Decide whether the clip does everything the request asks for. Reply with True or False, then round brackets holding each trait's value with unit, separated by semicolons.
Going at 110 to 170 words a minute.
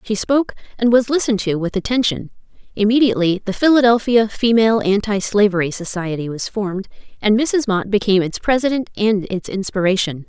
True (150 wpm)